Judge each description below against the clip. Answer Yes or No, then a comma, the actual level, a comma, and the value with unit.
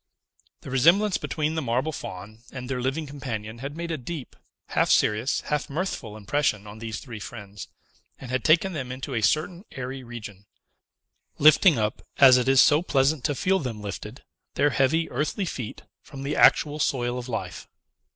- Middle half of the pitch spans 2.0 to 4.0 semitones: No, average, 4.6 semitones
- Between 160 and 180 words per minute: Yes, average, 175 wpm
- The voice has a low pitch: Yes, low, 130 Hz